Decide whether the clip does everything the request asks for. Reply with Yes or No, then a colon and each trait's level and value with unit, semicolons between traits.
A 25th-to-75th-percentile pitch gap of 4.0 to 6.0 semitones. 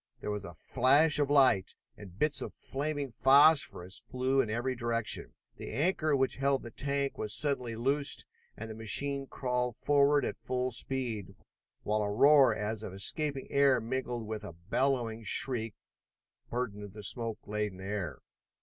Yes: average, 4.5 semitones